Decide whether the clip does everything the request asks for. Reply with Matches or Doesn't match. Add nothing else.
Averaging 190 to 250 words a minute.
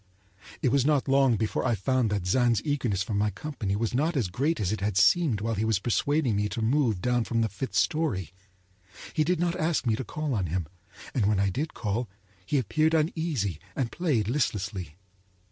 Matches